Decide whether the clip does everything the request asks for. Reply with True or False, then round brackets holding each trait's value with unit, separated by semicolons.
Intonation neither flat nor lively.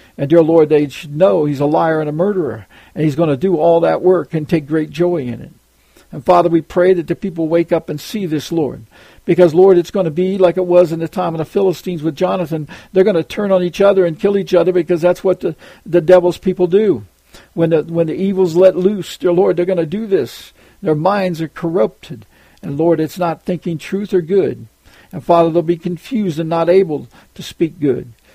False (2.3 semitones)